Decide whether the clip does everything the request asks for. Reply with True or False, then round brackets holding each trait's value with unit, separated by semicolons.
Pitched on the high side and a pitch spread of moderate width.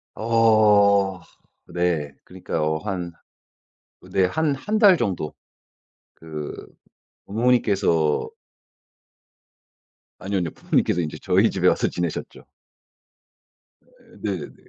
False (95 Hz; 4.6 semitones)